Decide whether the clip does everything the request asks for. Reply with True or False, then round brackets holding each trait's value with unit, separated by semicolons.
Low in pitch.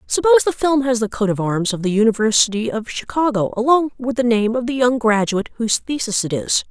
False (235 Hz)